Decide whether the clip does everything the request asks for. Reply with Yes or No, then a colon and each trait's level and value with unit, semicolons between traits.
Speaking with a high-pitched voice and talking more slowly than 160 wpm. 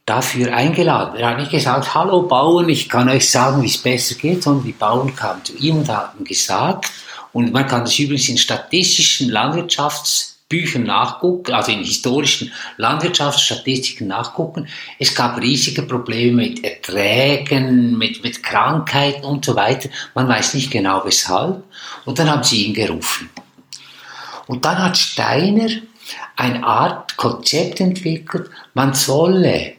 No: low, 135 Hz; average, 145 wpm